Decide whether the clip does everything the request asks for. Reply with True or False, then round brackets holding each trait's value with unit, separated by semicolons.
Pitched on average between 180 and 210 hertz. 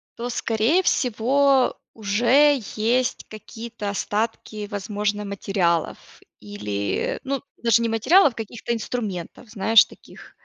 False (225 Hz)